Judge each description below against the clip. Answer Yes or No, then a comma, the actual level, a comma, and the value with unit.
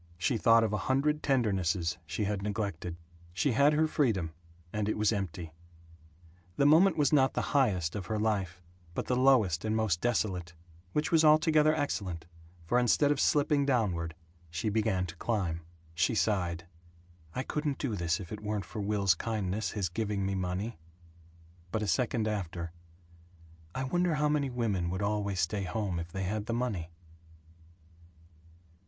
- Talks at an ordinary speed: Yes, average, 165 wpm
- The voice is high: No, low, 105 Hz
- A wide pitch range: Yes, wide, 5.8 semitones